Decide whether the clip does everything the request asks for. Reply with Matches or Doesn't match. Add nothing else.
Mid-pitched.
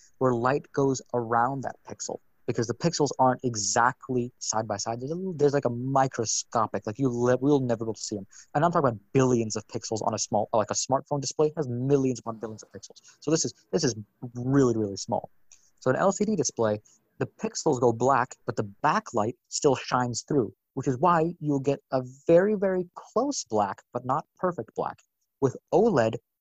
Doesn't match